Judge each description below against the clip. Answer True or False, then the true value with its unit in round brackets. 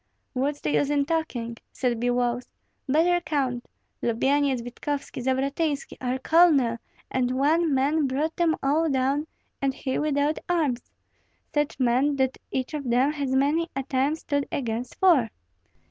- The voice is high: True (275 Hz)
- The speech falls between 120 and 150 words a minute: True (145 wpm)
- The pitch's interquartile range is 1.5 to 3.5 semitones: True (2.9 semitones)